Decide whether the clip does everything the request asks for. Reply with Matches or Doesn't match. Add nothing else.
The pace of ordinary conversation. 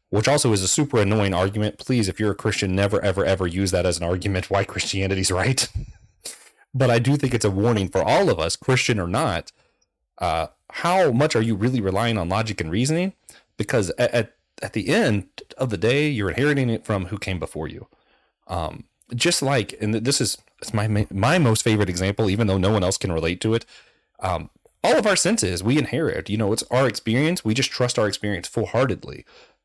Doesn't match